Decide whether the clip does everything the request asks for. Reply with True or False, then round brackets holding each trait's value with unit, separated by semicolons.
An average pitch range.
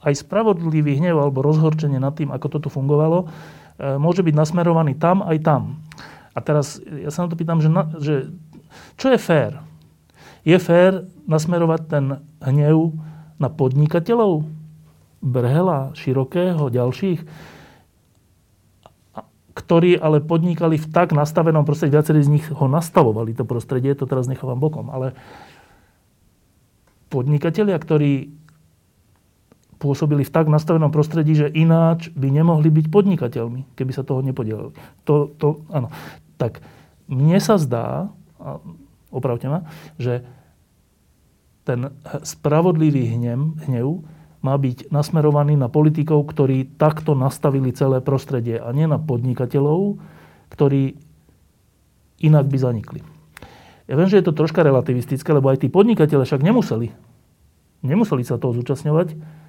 True (3.2 semitones)